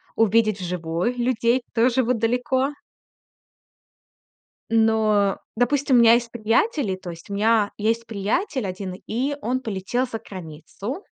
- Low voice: No, high, 225 Hz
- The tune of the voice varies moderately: Yes, average, 3.7 semitones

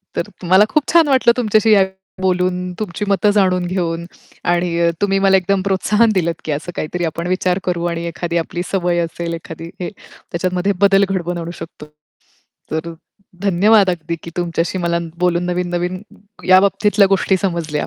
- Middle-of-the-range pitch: Yes, medium, 180 Hz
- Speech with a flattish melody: Yes, narrow, 2.3 semitones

